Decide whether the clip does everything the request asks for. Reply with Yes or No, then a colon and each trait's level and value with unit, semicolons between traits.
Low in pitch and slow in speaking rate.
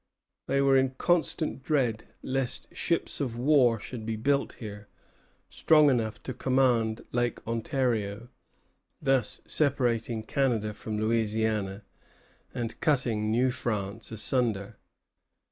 Yes: low, 120 Hz; slow, 110 wpm